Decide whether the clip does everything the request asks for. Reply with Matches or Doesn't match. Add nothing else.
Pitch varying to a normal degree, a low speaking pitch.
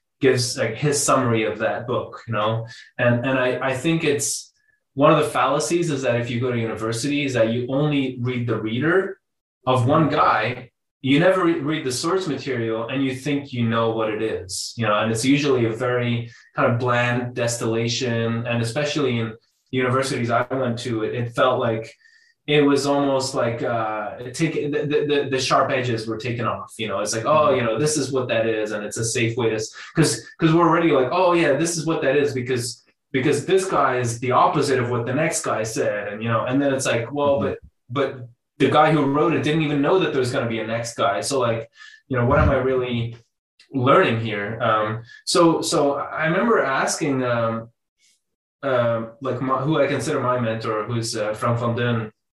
Matches